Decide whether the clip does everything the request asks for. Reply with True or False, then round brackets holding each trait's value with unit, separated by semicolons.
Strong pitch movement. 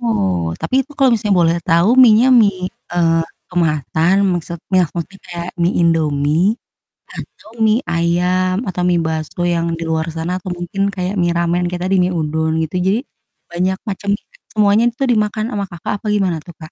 False (3.2 semitones)